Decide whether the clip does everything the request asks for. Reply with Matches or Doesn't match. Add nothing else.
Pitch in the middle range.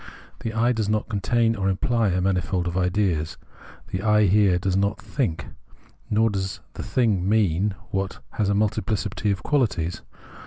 Doesn't match